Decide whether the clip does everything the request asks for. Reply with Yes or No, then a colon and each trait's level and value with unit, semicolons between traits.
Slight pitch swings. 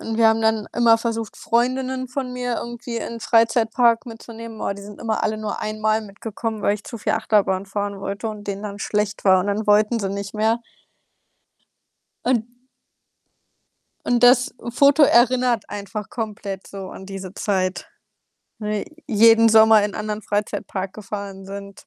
Yes: narrow, 2.3 semitones